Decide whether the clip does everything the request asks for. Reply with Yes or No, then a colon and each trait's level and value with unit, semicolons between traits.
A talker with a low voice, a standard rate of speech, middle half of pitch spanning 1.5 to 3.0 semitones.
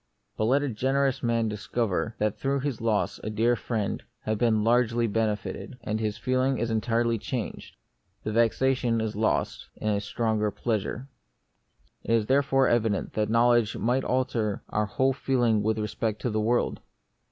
Yes: low, 115 Hz; average, 165 wpm; narrow, 2.5 semitones